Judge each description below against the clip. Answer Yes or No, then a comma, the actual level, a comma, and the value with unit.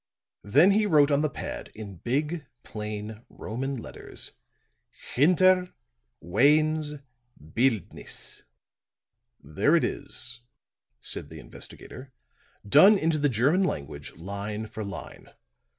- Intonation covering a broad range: Yes, wide, 6.5 semitones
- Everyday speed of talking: No, slow, 105 wpm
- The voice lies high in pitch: No, low, 135 Hz